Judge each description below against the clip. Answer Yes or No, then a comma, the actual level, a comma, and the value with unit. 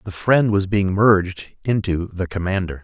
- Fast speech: No, average, 170 wpm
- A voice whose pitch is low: Yes, very low, 95 Hz